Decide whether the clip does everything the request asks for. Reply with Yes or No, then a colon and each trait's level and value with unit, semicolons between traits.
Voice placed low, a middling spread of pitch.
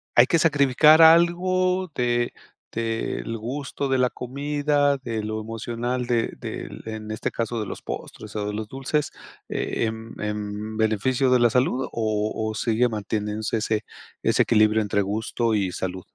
Yes: low, 115 Hz; average, 3.6 semitones